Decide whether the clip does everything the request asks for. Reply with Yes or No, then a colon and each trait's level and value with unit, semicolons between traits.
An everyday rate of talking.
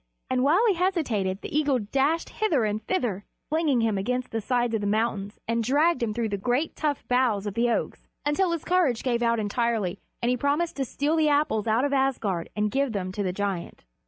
No: fast, 215 wpm